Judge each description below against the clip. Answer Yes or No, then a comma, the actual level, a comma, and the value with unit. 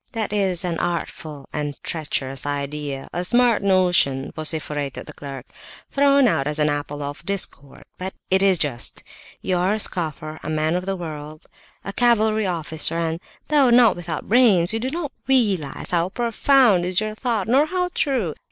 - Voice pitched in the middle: Yes, medium, 180 Hz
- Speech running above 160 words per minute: Yes, average, 170 wpm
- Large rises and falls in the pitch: Yes, wide, 6.5 semitones